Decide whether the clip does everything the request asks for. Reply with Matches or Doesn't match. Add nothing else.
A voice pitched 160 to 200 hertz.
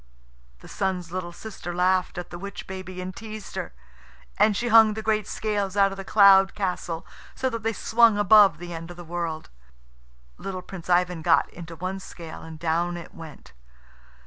Matches